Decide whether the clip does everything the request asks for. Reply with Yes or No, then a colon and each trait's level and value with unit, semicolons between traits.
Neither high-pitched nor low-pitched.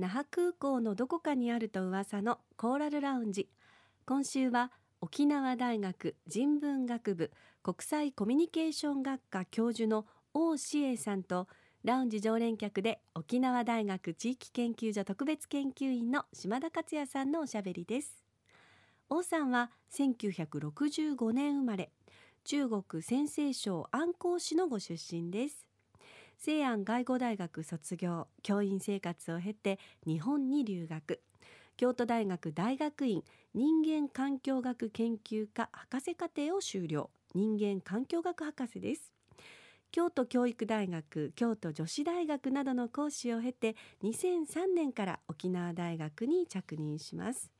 No: high, 240 Hz